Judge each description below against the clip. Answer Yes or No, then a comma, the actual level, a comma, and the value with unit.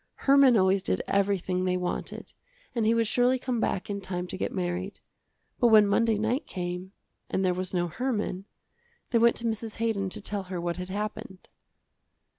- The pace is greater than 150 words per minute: Yes, average, 185 wpm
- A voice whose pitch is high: Yes, high, 200 Hz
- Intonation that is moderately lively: Yes, average, 3.7 semitones